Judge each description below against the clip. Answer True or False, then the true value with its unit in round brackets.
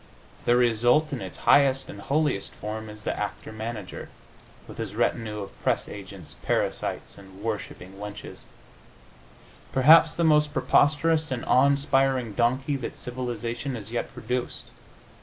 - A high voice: False (120 Hz)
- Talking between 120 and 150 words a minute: True (140 wpm)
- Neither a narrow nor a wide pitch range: True (4.4 semitones)